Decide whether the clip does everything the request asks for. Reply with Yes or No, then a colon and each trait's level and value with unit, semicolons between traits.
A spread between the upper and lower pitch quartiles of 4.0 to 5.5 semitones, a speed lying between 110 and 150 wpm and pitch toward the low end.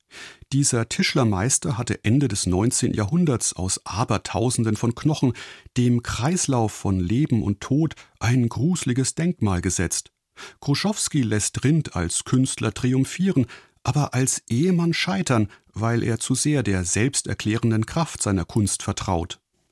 Yes: average, 4.8 semitones; slow, 125 wpm; low, 120 Hz